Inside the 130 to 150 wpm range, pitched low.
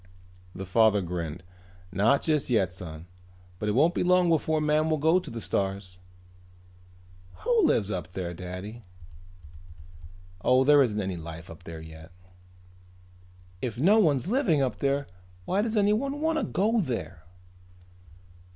Yes: average, 145 wpm; low, 120 Hz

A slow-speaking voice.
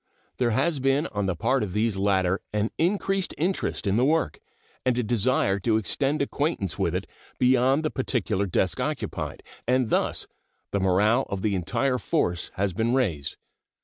No: average, 170 wpm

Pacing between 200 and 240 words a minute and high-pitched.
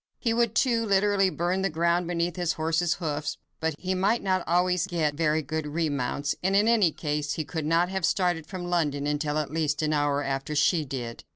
No: fast, 205 wpm; medium, 165 Hz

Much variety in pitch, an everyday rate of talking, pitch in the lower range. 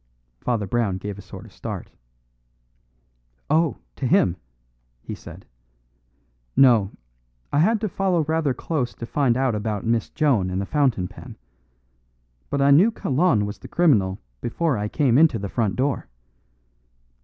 Yes: wide, 6.8 semitones; average, 150 wpm; low, 125 Hz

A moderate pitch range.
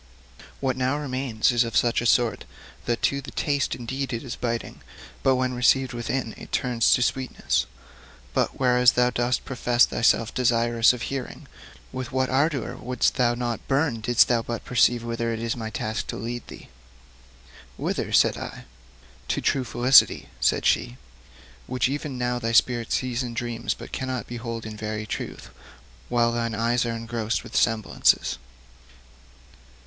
No: narrow, 1.7 semitones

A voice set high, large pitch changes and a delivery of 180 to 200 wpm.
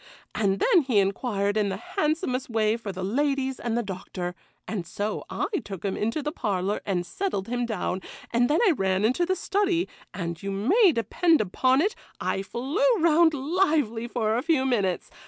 Yes: high, 235 Hz; wide, 7.2 semitones; average, 185 wpm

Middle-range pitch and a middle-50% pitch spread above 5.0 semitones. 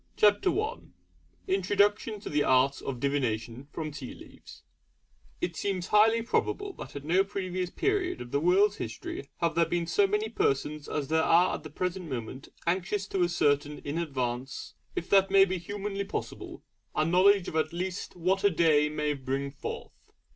Yes: medium, 170 Hz; wide, 5.5 semitones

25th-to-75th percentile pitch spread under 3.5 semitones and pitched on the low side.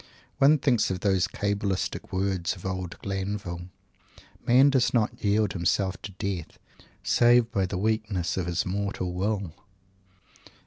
Yes: average, 2.9 semitones; low, 100 Hz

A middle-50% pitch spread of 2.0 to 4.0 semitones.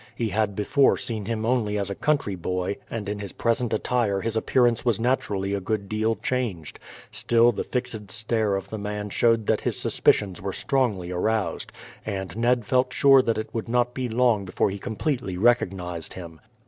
Yes: average, 3.5 semitones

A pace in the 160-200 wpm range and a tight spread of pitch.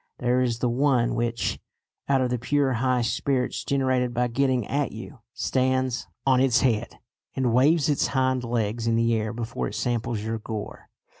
Yes: average, 175 wpm; narrow, 2.0 semitones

